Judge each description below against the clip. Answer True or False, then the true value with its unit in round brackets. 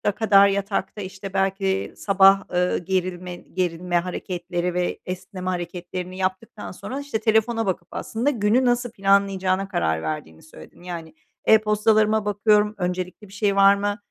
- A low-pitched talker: False (195 Hz)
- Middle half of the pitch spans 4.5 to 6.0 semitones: False (2.6 semitones)